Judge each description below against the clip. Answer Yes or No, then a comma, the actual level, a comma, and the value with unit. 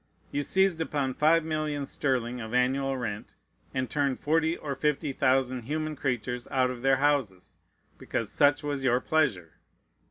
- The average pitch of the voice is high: No, low, 135 Hz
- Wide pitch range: No, average, 3.0 semitones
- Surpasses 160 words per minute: No, average, 155 wpm